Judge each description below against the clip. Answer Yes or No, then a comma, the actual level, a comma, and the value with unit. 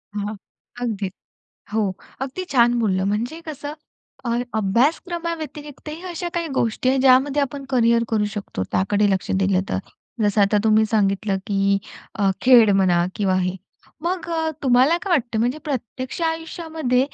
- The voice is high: Yes, high, 240 Hz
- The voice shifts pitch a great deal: Yes, wide, 6.4 semitones